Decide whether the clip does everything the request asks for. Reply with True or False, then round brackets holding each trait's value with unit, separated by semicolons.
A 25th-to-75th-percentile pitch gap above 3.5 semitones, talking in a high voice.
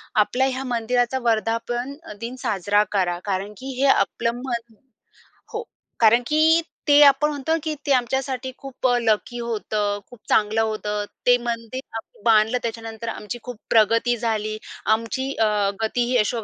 False (3.1 semitones; 230 Hz)